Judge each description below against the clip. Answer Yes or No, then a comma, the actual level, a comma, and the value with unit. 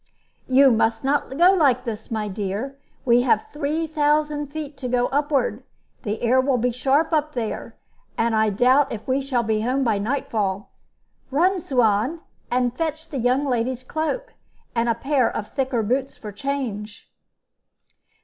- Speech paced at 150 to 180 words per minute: Yes, average, 165 wpm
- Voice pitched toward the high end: Yes, very high, 255 Hz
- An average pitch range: Yes, average, 4.0 semitones